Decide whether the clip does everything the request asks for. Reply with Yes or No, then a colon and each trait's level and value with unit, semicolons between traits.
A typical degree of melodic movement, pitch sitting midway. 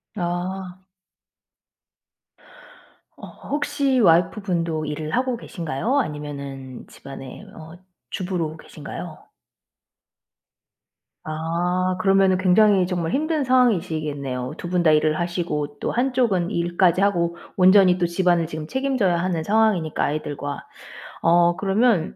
Yes: average, 3.9 semitones; medium, 175 Hz